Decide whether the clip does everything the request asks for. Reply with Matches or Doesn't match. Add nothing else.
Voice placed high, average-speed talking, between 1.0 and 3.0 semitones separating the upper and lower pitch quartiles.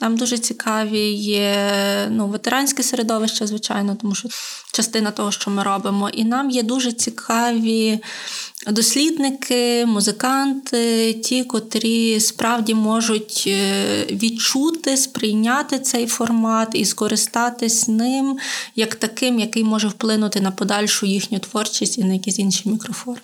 Matches